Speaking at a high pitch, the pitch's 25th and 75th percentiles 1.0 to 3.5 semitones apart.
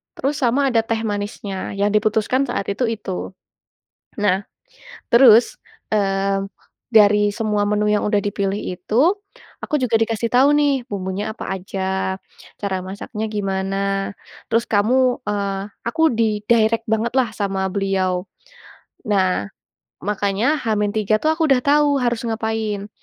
Yes: high, 210 Hz; average, 3.0 semitones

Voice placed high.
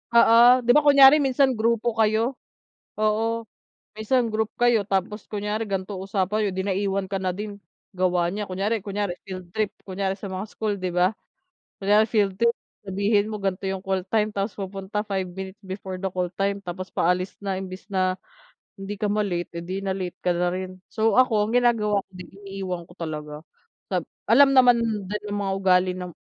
Yes: high, 200 Hz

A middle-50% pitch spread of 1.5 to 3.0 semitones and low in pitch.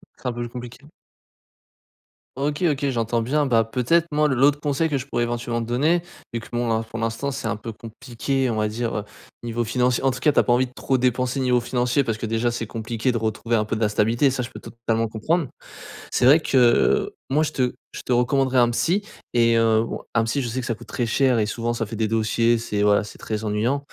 Yes: average, 2.7 semitones; low, 120 Hz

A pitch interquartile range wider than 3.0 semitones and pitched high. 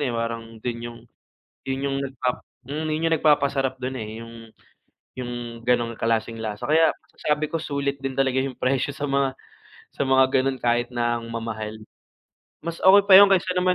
No: average, 3.5 semitones; low, 130 Hz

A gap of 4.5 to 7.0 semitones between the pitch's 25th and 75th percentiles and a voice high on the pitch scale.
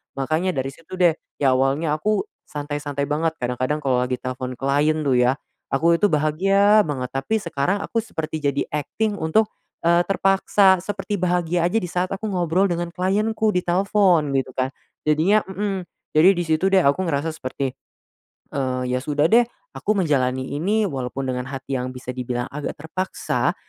No: wide, 5.6 semitones; medium, 160 Hz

